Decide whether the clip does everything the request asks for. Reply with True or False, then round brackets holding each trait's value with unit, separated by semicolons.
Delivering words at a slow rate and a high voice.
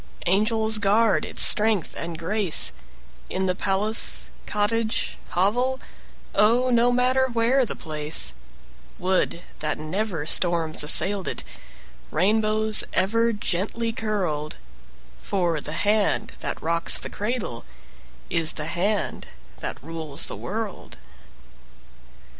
True (110 wpm; 205 Hz)